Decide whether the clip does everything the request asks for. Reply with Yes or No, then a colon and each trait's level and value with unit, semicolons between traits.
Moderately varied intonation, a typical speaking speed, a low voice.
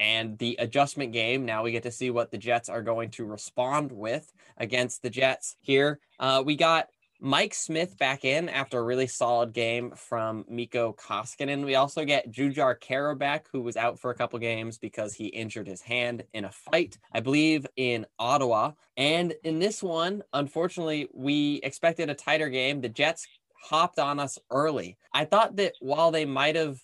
Yes: average, 3.8 semitones; average, 185 wpm; low, 130 Hz